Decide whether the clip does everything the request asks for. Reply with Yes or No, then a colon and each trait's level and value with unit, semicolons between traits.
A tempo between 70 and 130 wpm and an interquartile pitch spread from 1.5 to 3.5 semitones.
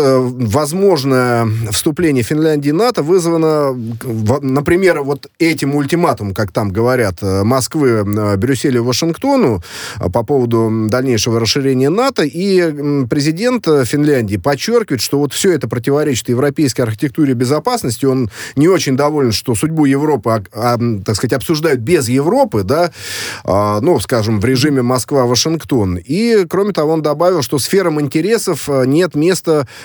No: average, 125 wpm; average, 5.0 semitones